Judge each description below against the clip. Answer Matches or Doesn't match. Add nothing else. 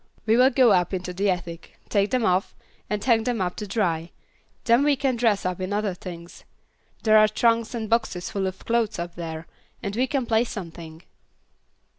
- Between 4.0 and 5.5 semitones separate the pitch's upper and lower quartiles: Matches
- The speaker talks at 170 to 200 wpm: Matches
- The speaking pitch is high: Matches